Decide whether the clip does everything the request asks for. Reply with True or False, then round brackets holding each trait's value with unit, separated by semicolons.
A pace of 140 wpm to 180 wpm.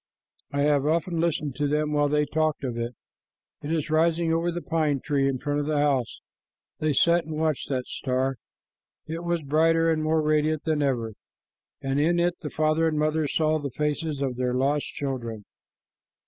False (190 wpm)